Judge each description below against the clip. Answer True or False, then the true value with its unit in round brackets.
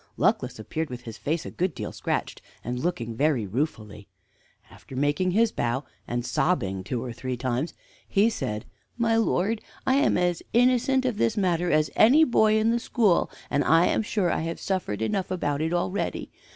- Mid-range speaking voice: True (165 Hz)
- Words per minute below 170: False (185 wpm)